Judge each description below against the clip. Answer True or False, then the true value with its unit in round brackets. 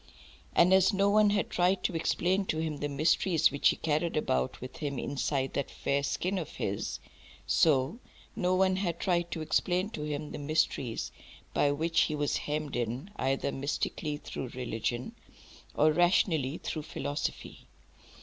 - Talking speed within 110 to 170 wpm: True (160 wpm)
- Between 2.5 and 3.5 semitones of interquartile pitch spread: False (4.0 semitones)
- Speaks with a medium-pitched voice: True (155 Hz)